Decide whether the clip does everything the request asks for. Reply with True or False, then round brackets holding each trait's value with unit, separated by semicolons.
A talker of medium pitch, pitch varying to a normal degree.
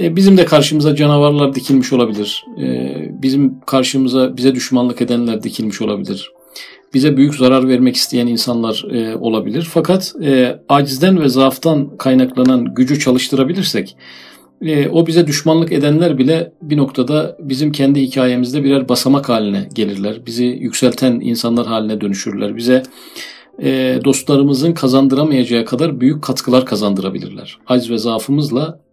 False (130 Hz; 3.1 semitones)